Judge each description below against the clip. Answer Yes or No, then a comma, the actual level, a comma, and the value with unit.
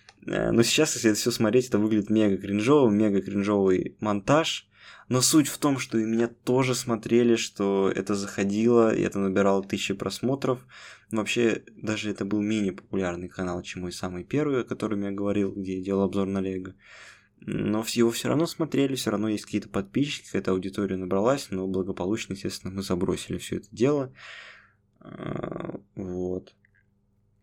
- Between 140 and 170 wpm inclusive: Yes, fast, 160 wpm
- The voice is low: Yes, low, 105 Hz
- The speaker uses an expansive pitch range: No, average, 3.3 semitones